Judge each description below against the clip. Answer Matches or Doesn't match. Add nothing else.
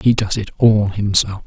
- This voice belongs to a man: Matches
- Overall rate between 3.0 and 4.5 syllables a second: Matches